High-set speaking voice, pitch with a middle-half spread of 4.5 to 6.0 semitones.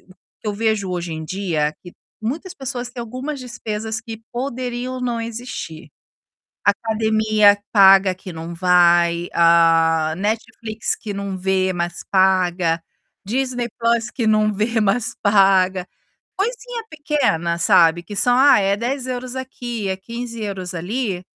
Yes: high, 210 Hz; average, 4.9 semitones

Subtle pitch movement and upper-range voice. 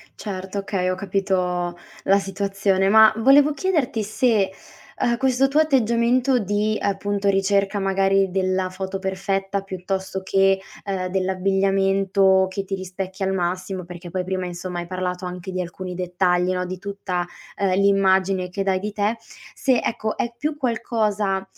Yes: narrow, 1.7 semitones; high, 195 Hz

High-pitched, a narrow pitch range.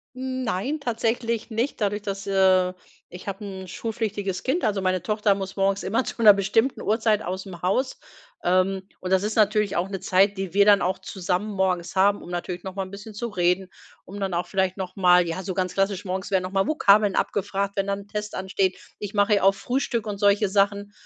Yes: high, 195 Hz; narrow, 1.9 semitones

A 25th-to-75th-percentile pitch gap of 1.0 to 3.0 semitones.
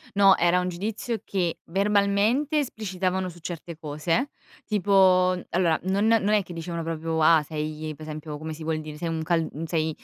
No: average, 3.8 semitones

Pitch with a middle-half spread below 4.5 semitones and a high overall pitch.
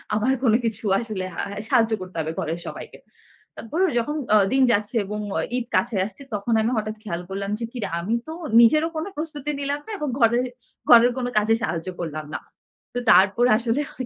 Yes: average, 4.1 semitones; high, 225 Hz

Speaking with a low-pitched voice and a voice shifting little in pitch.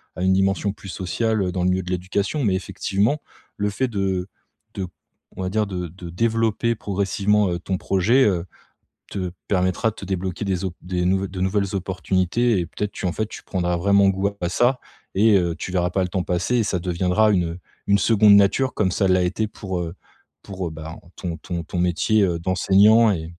Yes: very low, 95 Hz; narrow, 2.3 semitones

